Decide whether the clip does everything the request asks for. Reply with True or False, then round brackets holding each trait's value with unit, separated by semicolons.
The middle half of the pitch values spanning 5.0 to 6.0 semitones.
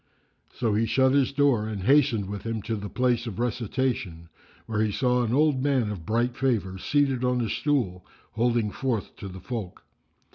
False (3.7 semitones)